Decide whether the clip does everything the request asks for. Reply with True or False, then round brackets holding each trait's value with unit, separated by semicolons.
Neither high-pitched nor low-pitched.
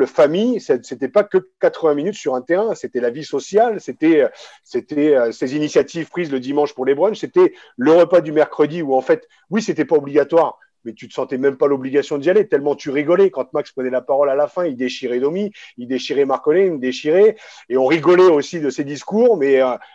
True (155 Hz)